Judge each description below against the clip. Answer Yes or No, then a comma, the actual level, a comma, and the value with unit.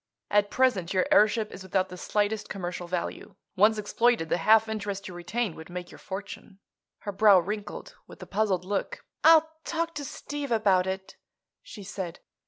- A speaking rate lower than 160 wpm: No, average, 175 wpm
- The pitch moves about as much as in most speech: Yes, average, 3.0 semitones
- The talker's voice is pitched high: Yes, high, 205 Hz